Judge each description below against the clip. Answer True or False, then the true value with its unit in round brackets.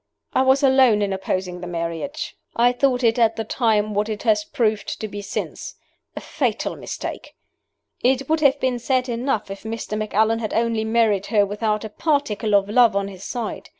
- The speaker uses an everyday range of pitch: True (3.3 semitones)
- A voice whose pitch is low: False (220 Hz)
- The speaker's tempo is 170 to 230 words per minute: True (190 wpm)